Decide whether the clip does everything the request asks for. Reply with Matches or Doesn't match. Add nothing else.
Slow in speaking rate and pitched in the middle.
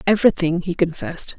Matches